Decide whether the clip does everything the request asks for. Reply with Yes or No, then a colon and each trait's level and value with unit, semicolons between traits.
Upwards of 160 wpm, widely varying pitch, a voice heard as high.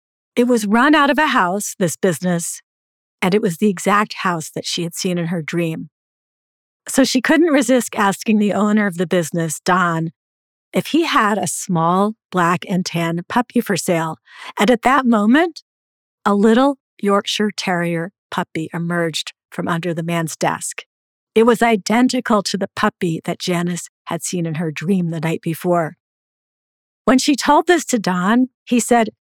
Yes: average, 170 wpm; wide, 5.7 semitones; high, 195 Hz